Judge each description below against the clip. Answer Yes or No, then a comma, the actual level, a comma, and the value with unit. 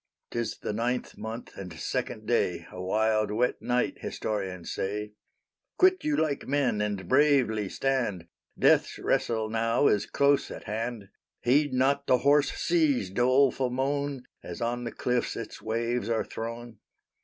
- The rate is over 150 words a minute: No, average, 145 wpm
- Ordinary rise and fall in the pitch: Yes, average, 4.1 semitones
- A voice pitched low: Yes, low, 120 Hz